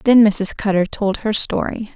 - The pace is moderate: Yes, average, 185 wpm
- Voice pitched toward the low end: No, high, 210 Hz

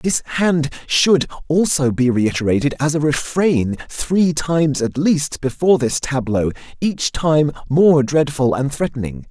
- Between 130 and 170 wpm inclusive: Yes, average, 140 wpm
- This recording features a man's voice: Yes, male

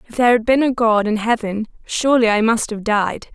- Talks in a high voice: Yes, high, 225 Hz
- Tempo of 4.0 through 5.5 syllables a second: No, 5.8 syllables/s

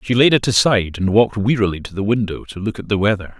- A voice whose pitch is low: Yes, low, 105 Hz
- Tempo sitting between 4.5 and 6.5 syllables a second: No, 6.8 syllables/s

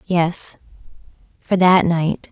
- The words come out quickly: No, slow, 105 wpm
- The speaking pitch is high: No, medium, 175 Hz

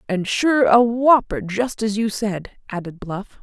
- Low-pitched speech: No, high, 220 Hz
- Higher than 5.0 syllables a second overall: No, 4.0 syllables/s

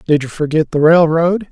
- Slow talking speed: No, average, 200 wpm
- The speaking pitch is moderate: Yes, medium, 160 Hz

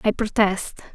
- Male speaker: No, female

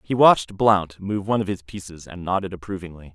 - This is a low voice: Yes, very low, 95 Hz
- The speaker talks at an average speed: No, fast, 210 wpm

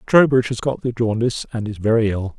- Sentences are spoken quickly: Yes, fast, 225 wpm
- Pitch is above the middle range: No, low, 115 Hz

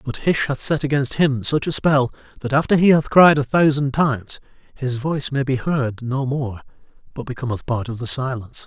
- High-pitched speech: No, low, 135 Hz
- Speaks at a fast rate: Yes, fast, 210 wpm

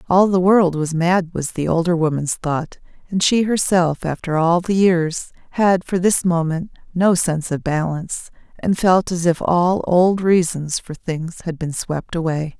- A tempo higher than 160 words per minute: Yes, average, 180 wpm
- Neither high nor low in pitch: Yes, medium, 175 Hz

